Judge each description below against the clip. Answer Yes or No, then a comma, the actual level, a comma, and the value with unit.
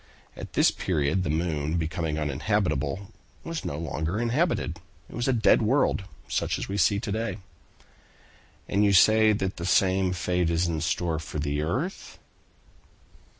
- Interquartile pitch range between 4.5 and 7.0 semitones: Yes, average, 5.2 semitones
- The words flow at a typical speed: Yes, average, 160 wpm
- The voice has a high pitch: No, very low, 90 Hz